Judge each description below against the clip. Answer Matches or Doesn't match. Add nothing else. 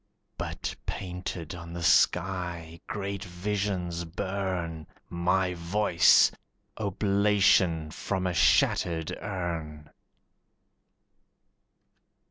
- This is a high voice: Doesn't match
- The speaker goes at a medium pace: Doesn't match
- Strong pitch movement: Doesn't match